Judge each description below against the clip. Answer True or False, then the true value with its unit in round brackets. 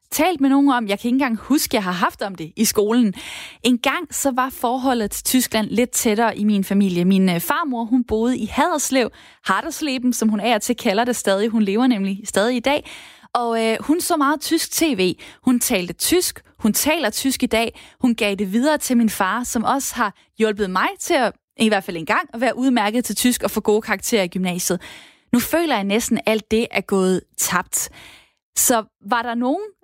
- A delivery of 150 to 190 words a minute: False (215 wpm)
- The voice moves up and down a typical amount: True (4.1 semitones)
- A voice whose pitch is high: True (235 Hz)